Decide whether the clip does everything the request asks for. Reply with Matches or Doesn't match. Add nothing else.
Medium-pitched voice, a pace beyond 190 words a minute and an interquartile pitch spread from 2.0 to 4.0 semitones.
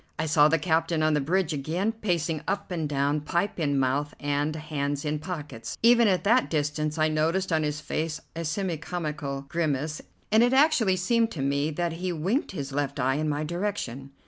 Matches